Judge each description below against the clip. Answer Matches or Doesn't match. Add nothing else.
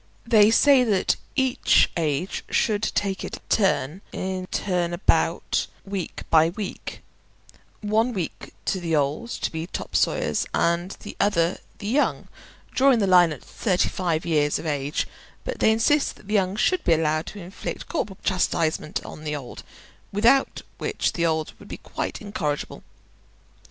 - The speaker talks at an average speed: Matches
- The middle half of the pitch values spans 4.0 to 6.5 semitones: Matches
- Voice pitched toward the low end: Doesn't match